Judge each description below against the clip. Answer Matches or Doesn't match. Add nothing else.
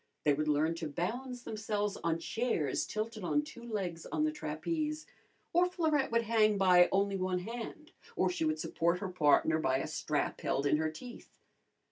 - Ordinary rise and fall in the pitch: Doesn't match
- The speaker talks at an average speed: Matches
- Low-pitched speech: Doesn't match